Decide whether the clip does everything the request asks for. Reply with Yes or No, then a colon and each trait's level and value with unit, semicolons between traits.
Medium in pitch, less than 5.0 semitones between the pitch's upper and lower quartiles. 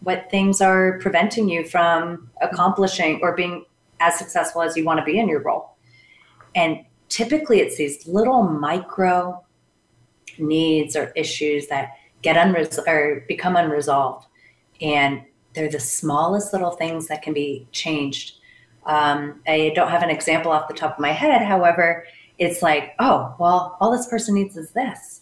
Yes: medium, 165 Hz; average, 3.5 semitones